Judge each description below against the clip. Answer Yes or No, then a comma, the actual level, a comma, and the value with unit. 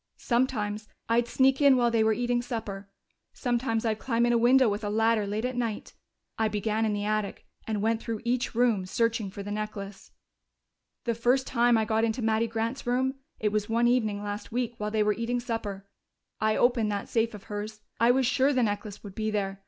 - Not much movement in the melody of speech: Yes, narrow, 2.3 semitones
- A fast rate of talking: Yes, fast, 210 wpm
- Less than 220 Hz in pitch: No, high, 225 Hz